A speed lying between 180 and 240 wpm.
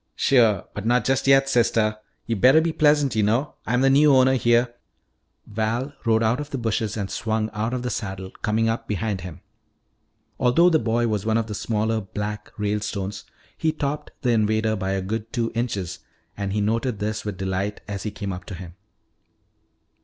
Yes: average, 195 wpm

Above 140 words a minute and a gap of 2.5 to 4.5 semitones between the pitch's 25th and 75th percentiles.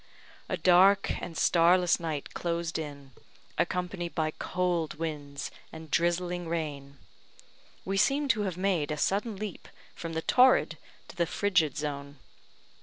No: slow, 135 wpm; average, 2.9 semitones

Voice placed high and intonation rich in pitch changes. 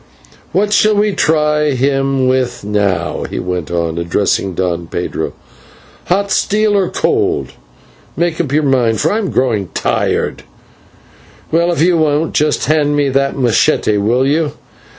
No: medium, 140 Hz; wide, 7.6 semitones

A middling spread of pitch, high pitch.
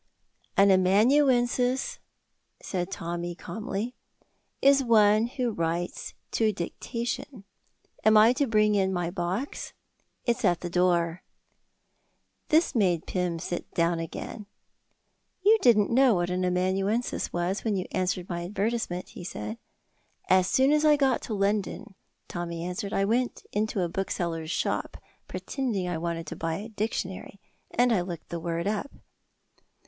Yes: average, 4.9 semitones; high, 195 Hz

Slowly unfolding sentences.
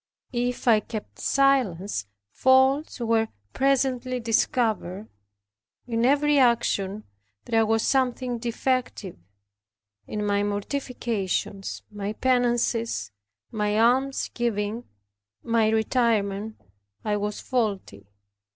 Yes: slow, 90 wpm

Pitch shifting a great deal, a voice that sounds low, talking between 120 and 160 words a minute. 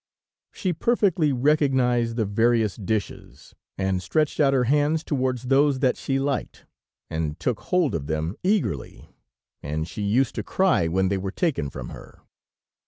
Yes: wide, 7.4 semitones; low, 125 Hz; average, 155 wpm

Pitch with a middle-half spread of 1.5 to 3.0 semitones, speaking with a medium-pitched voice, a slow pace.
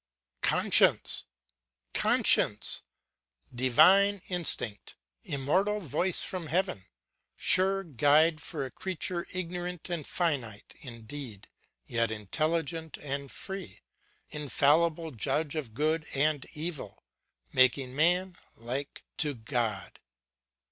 No: average, 5.2 semitones; medium, 150 Hz; slow, 95 wpm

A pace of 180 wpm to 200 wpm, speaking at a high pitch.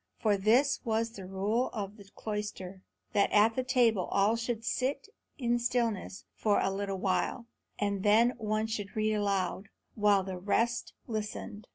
No: average, 160 wpm; high, 210 Hz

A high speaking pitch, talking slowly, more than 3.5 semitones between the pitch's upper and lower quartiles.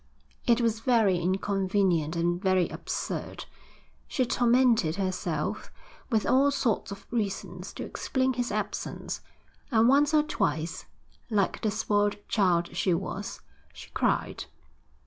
Yes: high, 205 Hz; slow, 125 wpm; average, 4.8 semitones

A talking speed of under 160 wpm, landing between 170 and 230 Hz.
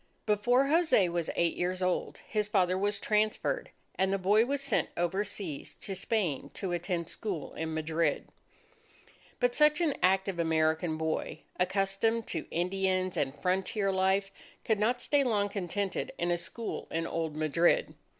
Yes: average, 150 wpm; high, 190 Hz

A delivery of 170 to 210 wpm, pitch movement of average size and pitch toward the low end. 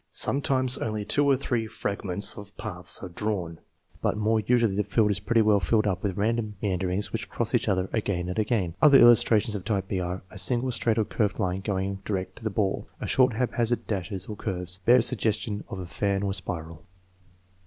Yes: average, 200 wpm; average, 3.0 semitones; low, 105 Hz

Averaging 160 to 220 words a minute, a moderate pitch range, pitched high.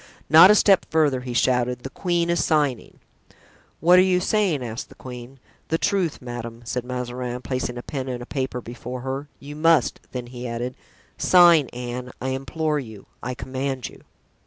No: average, 175 wpm; average, 4.2 semitones; low, 130 Hz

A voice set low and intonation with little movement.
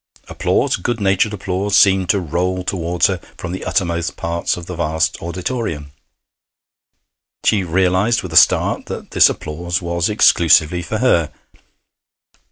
Yes: very low, 90 Hz; narrow, 2.3 semitones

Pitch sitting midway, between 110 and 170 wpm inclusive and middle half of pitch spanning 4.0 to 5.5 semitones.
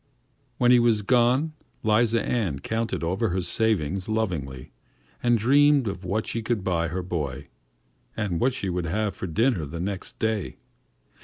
No: low, 105 Hz; average, 165 wpm; average, 4.9 semitones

